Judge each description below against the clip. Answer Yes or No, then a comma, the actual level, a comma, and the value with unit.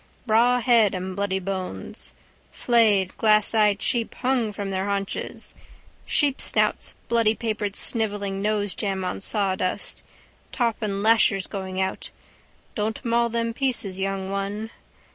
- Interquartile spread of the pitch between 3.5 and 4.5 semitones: No, average, 2.8 semitones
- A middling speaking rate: No, slow, 110 wpm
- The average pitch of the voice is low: No, high, 205 Hz